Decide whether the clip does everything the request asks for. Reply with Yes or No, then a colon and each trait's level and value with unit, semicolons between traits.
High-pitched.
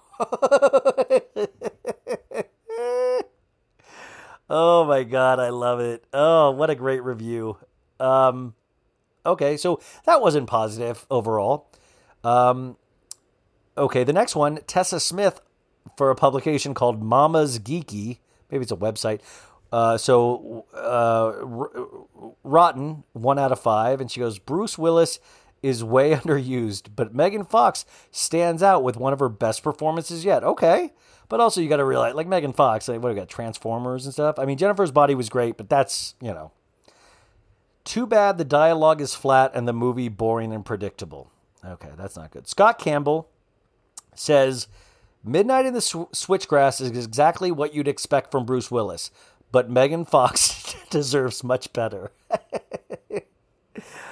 No: low, 135 Hz